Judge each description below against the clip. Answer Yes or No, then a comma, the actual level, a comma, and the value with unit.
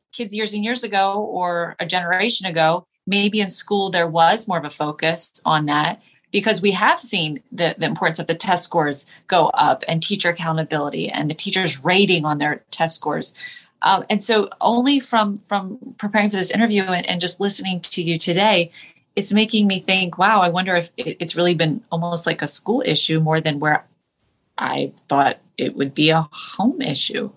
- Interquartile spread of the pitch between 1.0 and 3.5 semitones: No, average, 4.1 semitones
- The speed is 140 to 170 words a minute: No, average, 195 wpm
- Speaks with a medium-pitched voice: Yes, medium, 180 Hz